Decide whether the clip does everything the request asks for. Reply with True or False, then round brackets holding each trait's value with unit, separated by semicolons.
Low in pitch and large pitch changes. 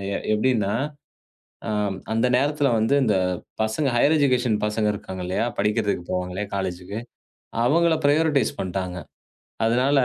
True (110 Hz; 6.0 semitones)